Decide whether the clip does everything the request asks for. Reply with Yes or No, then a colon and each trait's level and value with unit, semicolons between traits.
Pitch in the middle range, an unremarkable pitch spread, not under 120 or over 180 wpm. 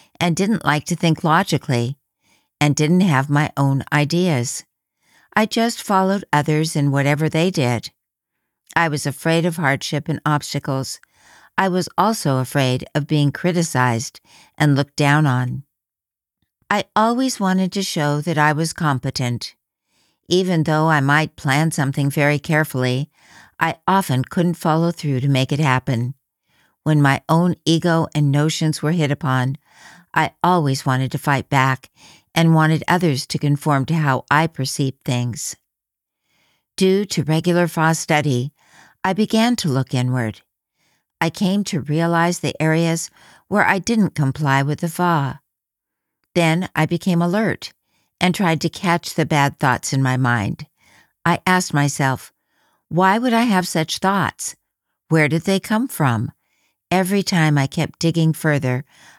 Yes: medium, 155 Hz; average, 3.7 semitones; average, 150 wpm